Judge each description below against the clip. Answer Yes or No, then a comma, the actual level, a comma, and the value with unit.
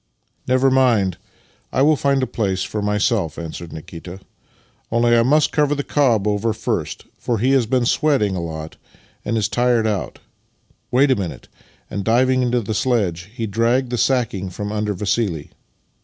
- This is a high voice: No, low, 115 Hz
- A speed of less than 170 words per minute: No, average, 180 wpm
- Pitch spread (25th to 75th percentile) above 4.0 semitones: Yes, average, 4.8 semitones